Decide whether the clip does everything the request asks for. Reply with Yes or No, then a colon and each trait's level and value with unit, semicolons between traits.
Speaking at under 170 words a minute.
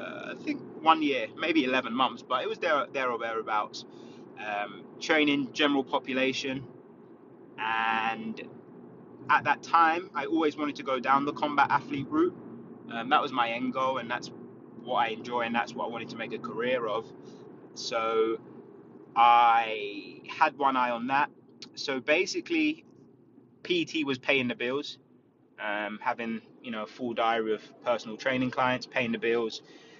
Yes: average, 155 wpm